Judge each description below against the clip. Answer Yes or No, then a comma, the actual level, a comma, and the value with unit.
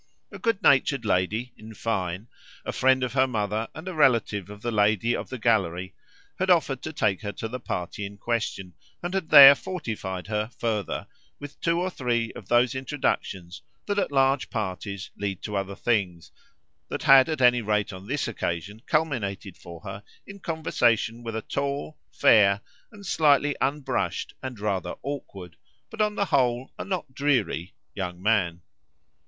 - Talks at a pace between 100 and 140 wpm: No, average, 170 wpm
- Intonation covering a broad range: Yes, wide, 5.9 semitones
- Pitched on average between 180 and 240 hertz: No, low, 115 Hz